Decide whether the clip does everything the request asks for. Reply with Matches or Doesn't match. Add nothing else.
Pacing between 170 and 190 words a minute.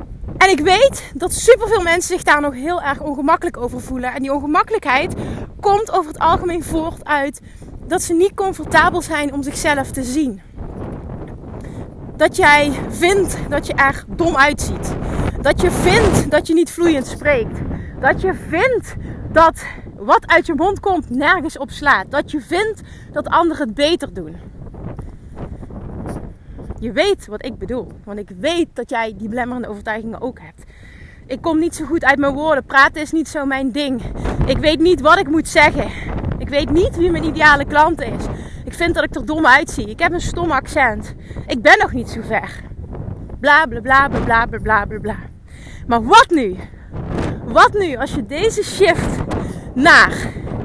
Matches